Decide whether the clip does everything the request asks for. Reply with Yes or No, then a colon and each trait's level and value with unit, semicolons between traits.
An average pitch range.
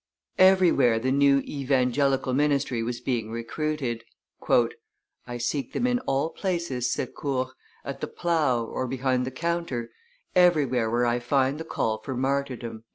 Yes: average, 3.4 semitones